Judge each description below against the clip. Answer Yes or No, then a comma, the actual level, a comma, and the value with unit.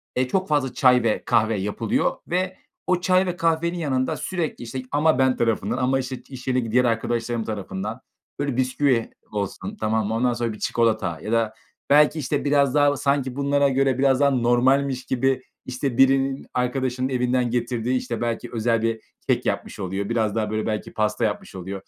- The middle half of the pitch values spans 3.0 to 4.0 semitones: Yes, average, 3.4 semitones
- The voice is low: Yes, low, 125 Hz